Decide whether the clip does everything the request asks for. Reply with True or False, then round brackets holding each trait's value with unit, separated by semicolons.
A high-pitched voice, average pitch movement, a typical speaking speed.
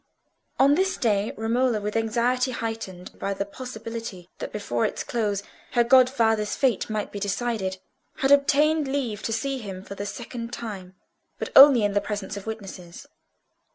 True (225 Hz; 3.9 semitones; 160 wpm)